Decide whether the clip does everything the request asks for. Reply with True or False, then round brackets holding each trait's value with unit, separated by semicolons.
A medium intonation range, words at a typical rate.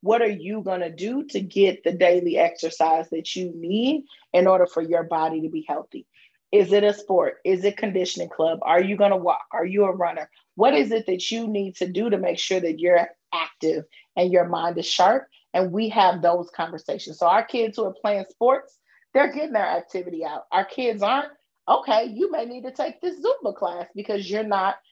False (4.2 semitones; 215 wpm)